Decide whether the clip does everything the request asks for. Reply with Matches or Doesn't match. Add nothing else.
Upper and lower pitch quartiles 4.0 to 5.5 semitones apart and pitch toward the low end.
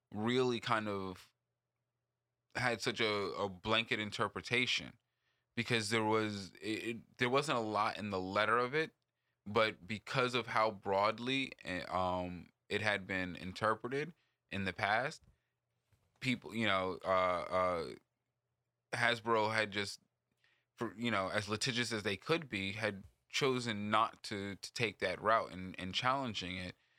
Doesn't match